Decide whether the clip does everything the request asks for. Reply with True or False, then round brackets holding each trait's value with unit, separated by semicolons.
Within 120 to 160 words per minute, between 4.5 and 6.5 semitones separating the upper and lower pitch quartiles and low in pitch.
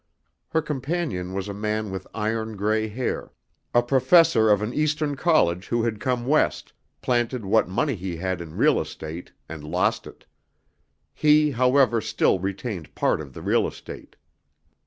True (155 wpm; 5.4 semitones; 110 Hz)